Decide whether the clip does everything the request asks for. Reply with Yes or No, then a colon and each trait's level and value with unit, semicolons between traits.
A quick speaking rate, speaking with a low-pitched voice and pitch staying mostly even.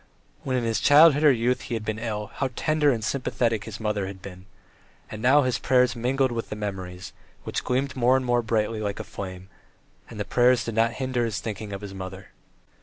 No: fast, 215 wpm; low, 115 Hz; average, 3.6 semitones